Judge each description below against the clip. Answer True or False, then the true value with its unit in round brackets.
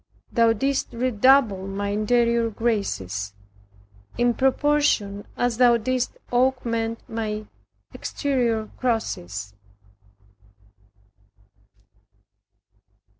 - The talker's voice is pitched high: True (230 Hz)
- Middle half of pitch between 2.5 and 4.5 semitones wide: True (3.4 semitones)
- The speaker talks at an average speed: False (70 wpm)